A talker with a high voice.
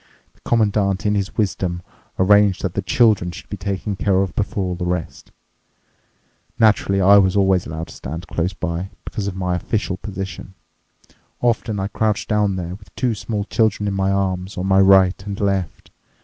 No: very low, 95 Hz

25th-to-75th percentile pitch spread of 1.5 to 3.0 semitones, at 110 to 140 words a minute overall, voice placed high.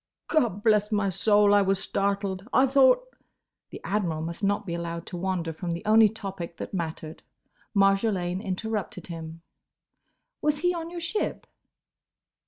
No: average, 4.1 semitones; slow, 135 wpm; high, 195 Hz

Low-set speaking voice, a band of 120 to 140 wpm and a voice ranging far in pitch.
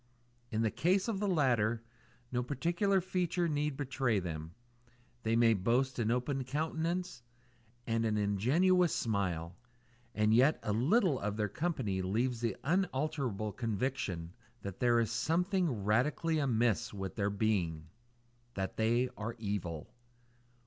Yes: low, 120 Hz; slow, 135 wpm; wide, 6.4 semitones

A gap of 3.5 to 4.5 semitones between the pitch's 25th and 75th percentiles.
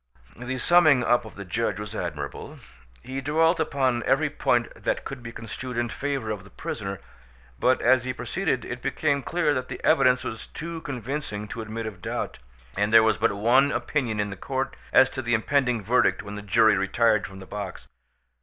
Yes: average, 3.8 semitones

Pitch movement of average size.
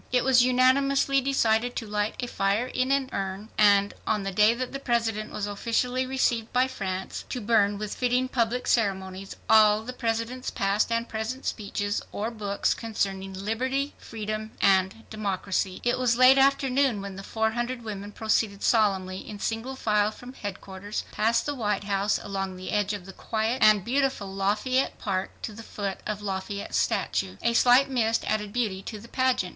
Yes: average, 3.7 semitones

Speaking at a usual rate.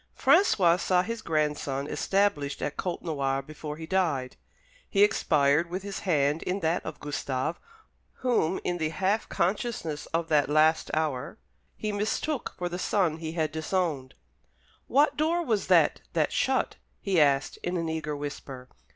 Yes: average, 150 wpm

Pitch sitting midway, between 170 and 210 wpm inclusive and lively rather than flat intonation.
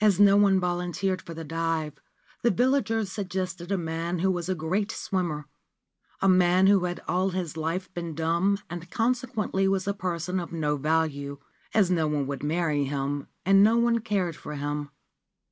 No: medium, 175 Hz; average, 180 wpm; average, 3.3 semitones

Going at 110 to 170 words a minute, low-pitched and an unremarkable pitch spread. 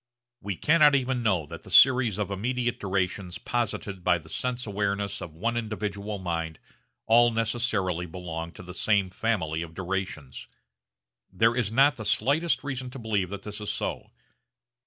Yes: average, 160 wpm; low, 105 Hz; average, 4.6 semitones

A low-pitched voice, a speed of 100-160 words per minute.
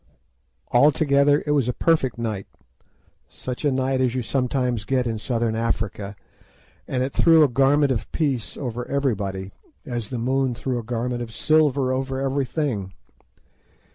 Yes: low, 130 Hz; average, 150 wpm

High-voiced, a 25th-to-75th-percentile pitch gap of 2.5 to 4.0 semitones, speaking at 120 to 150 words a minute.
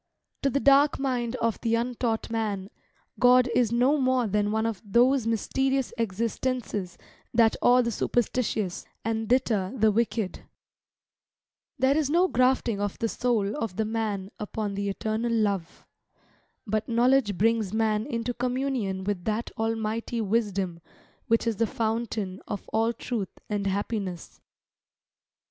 Yes: high, 225 Hz; average, 3.0 semitones; average, 140 wpm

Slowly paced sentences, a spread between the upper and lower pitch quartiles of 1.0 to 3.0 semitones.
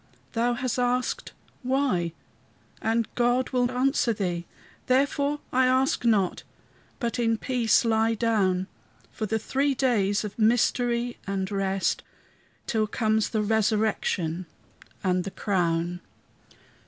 No: slow, 115 wpm; average, 3.9 semitones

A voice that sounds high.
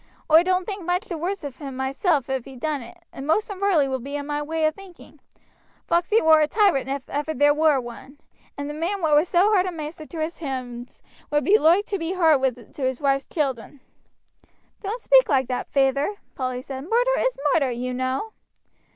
Yes: very high, 300 Hz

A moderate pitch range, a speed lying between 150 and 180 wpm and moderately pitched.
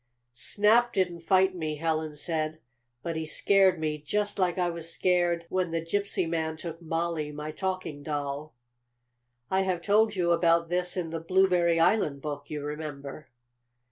Yes: average, 3.0 semitones; average, 160 wpm; medium, 165 Hz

